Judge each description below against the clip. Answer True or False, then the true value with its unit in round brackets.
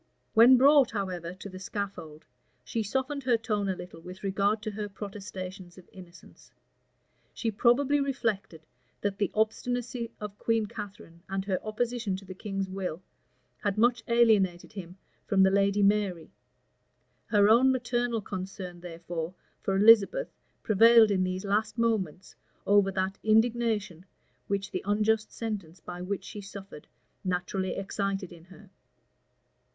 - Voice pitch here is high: True (200 Hz)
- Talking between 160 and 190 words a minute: False (140 wpm)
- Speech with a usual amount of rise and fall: True (3.0 semitones)